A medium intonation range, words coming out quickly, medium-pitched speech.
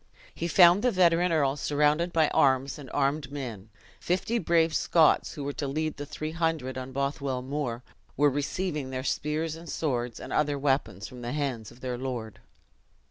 No: average, 3.6 semitones; average, 180 wpm; medium, 145 Hz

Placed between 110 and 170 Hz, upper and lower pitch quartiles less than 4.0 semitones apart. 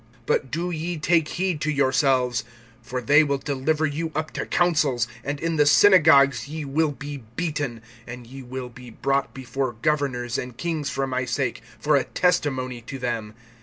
Yes: medium, 140 Hz; average, 3.5 semitones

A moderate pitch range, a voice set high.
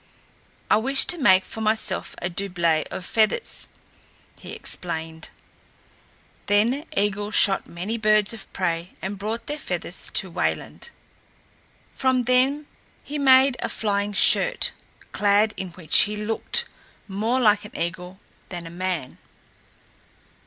Yes: average, 3.9 semitones; high, 205 Hz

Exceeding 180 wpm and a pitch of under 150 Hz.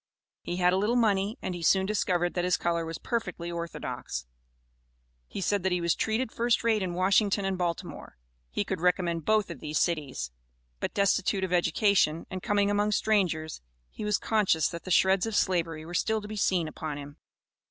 No: average, 195 wpm; medium, 185 Hz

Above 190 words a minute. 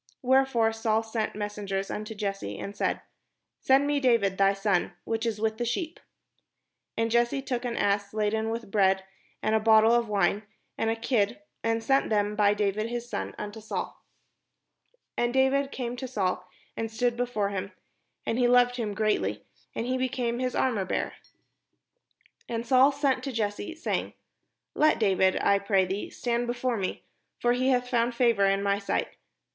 No: average, 170 wpm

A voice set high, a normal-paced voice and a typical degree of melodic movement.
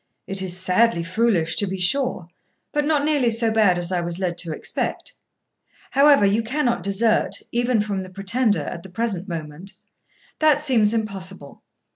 Yes: high, 205 Hz; average, 165 wpm; average, 4.5 semitones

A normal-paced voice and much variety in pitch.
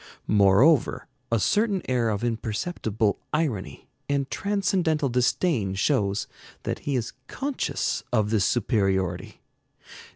No: slow, 105 wpm; wide, 7.1 semitones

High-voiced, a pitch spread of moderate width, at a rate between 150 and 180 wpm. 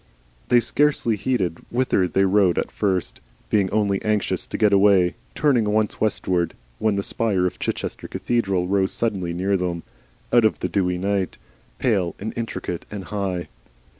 No: low, 100 Hz; average, 3.0 semitones; average, 160 wpm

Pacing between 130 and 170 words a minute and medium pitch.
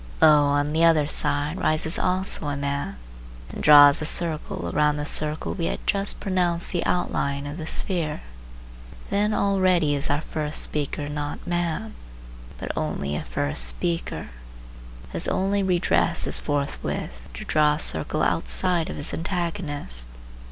Yes: average, 150 wpm; medium, 155 Hz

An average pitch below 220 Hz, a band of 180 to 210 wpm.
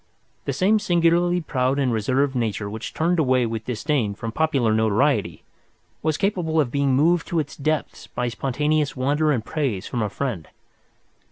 No: medium, 140 Hz; average, 165 wpm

